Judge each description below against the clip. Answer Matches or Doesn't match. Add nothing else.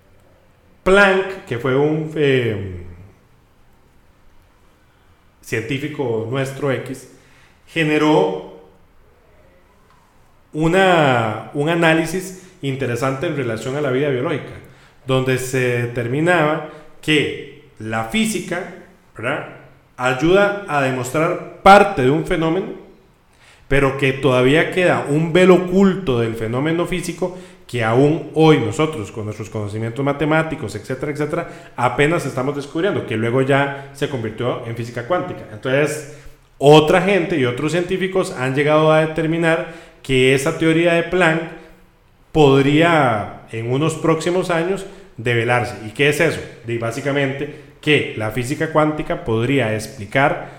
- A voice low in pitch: Doesn't match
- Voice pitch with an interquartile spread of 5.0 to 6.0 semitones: Matches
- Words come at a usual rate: Doesn't match